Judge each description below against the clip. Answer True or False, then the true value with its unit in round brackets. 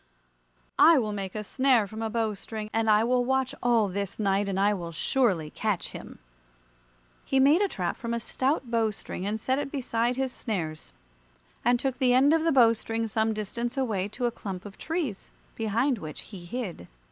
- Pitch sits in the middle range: False (225 Hz)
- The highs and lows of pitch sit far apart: False (4.0 semitones)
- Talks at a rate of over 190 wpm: True (200 wpm)